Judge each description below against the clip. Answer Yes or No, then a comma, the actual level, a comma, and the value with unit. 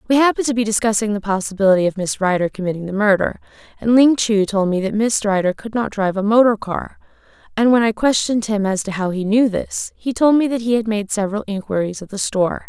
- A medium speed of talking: No, fast, 235 wpm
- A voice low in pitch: No, high, 210 Hz